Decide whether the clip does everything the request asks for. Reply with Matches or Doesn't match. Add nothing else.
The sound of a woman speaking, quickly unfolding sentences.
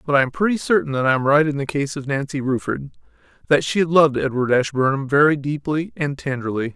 Doesn't match